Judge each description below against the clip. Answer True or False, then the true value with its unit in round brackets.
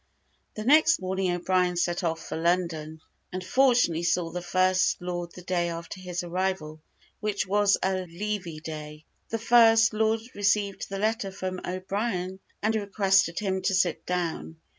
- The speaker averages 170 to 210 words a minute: False (155 wpm)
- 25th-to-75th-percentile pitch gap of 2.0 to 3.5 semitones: True (2.8 semitones)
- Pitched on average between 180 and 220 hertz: True (185 Hz)